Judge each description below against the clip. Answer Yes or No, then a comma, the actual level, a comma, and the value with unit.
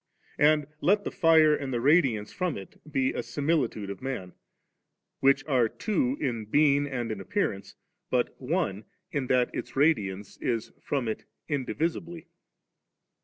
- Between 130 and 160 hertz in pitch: Yes, low, 135 Hz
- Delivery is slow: No, average, 150 wpm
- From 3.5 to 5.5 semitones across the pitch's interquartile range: Yes, average, 5.2 semitones